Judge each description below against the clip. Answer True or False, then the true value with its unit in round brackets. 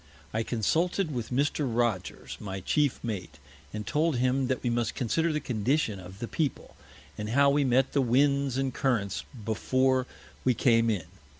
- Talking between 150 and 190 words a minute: True (170 wpm)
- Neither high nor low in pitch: False (125 Hz)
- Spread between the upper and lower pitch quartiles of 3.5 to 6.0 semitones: True (3.9 semitones)